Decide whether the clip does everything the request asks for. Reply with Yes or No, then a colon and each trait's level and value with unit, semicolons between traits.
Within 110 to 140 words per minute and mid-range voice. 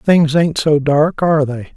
No: fast, 205 wpm; medium, 150 Hz